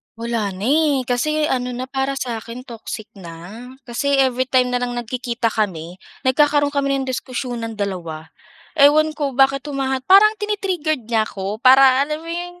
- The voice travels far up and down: No, average, 3.8 semitones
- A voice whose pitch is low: No, very high, 255 Hz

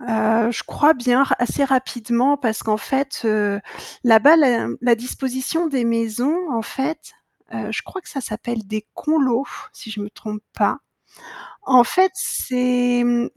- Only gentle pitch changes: No, average, 3.3 semitones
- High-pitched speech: Yes, high, 245 Hz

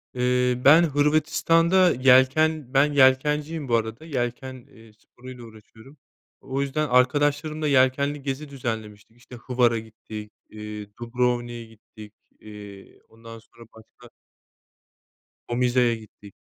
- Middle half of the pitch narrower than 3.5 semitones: No, average, 4.0 semitones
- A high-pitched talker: No, low, 125 Hz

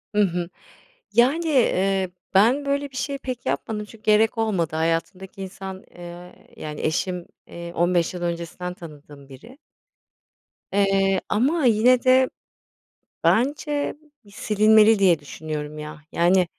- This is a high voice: Yes, high, 195 Hz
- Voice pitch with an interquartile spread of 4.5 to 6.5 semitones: Yes, average, 5.2 semitones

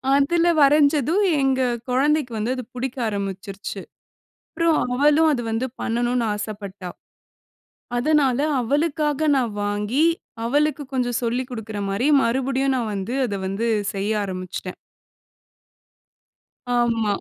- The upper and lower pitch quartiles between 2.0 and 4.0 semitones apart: No, average, 5.1 semitones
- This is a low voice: No, high, 245 Hz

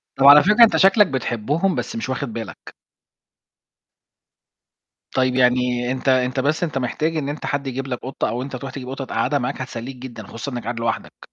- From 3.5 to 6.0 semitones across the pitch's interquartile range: No, narrow, 2.5 semitones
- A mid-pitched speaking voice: No, low, 130 Hz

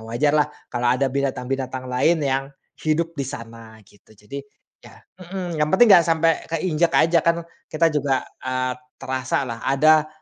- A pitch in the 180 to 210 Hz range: No, medium, 140 Hz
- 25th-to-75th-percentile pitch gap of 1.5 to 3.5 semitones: No, average, 4.3 semitones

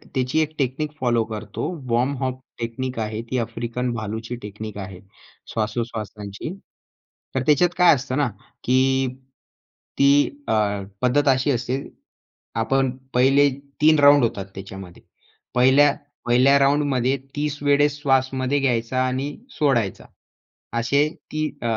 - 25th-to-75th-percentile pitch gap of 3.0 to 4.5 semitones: Yes, average, 3.6 semitones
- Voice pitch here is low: Yes, low, 130 Hz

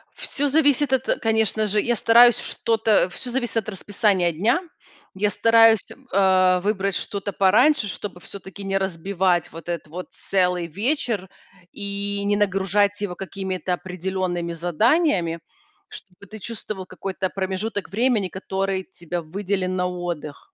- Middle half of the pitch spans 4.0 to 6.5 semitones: No, average, 3.0 semitones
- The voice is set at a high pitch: Yes, high, 195 Hz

